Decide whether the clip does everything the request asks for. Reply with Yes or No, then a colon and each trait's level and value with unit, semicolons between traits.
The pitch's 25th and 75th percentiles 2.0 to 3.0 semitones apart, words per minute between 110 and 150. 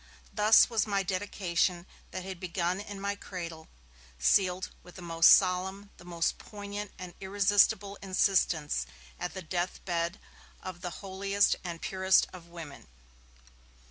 Yes: narrow, 2.5 semitones; average, 140 wpm